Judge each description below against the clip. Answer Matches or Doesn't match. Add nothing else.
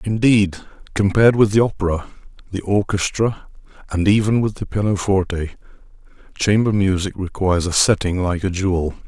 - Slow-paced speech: Matches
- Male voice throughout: Matches